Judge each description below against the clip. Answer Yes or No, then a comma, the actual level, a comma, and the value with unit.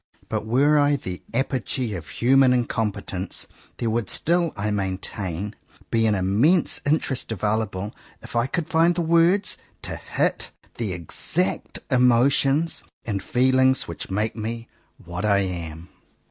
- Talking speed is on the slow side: Yes, slow, 130 wpm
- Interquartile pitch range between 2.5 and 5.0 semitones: No, wide, 5.4 semitones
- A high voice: No, low, 115 Hz